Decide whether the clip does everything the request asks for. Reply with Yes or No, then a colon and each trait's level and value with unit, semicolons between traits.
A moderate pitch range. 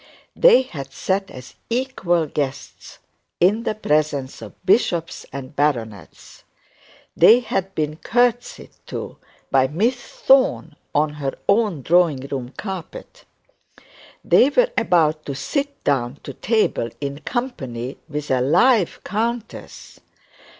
No: wide, 8.6 semitones